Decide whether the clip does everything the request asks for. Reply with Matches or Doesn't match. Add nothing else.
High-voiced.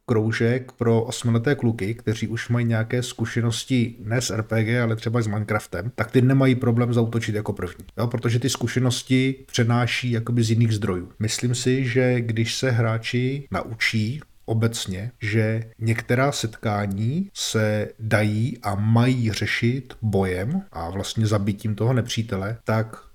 Doesn't match